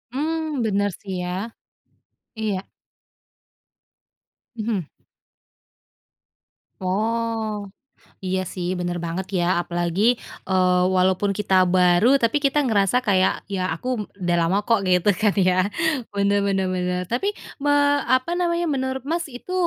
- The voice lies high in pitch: Yes, high, 200 Hz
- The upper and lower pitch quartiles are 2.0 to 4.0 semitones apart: No, average, 5.1 semitones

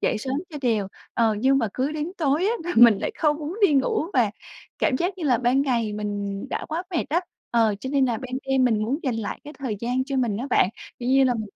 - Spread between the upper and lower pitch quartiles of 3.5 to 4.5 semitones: Yes, average, 4.2 semitones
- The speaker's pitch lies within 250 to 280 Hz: Yes, very high, 255 Hz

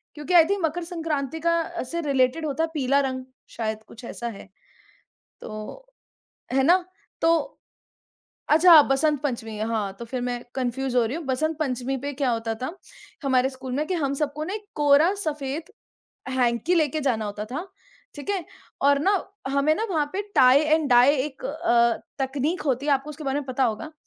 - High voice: Yes, very high, 280 Hz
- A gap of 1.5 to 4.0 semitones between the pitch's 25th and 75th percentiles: Yes, average, 3.7 semitones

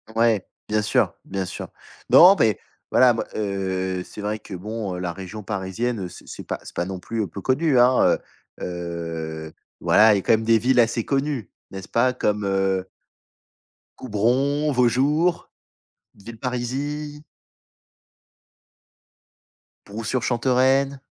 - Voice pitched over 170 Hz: No, low, 110 Hz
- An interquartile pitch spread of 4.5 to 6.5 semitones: Yes, average, 4.9 semitones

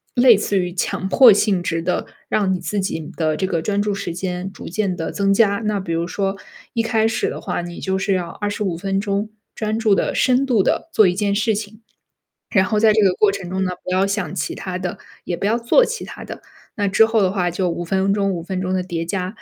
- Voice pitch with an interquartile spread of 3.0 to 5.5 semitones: No, narrow, 2.6 semitones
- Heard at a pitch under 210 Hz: Yes, high, 195 Hz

